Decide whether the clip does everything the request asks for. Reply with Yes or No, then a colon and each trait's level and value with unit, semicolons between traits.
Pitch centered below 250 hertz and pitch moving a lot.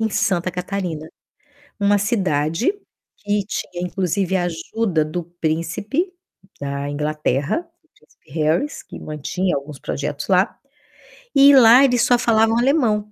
Yes: medium, 185 Hz; wide, 6.3 semitones